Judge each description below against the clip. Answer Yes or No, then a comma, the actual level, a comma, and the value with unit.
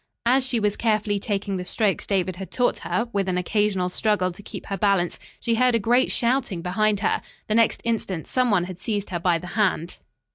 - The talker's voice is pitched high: Yes, high, 205 Hz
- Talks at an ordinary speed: No, fast, 215 wpm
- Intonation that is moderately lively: Yes, average, 3.6 semitones